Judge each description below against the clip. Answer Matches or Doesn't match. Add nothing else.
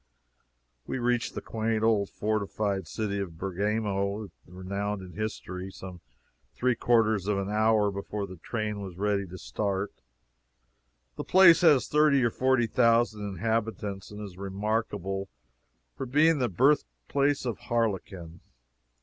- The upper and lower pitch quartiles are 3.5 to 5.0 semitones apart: Doesn't match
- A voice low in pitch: Matches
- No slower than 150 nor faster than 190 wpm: Doesn't match